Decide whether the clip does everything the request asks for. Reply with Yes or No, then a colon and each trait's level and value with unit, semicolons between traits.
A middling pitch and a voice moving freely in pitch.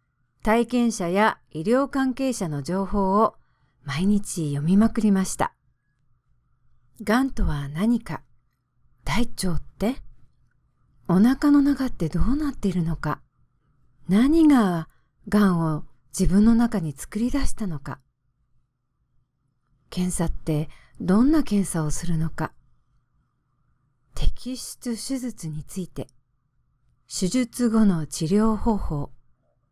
Yes: medium, 175 Hz; wide, 8.6 semitones